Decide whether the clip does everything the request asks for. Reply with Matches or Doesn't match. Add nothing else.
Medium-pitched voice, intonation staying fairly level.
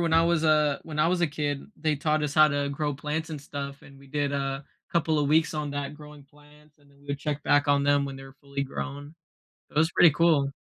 Matches